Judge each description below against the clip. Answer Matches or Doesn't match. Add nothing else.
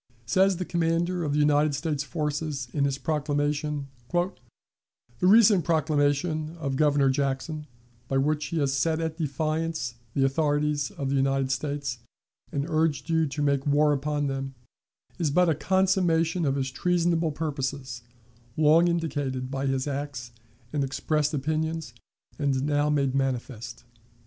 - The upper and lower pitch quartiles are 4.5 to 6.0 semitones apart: Doesn't match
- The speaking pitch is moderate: Matches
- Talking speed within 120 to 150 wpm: Matches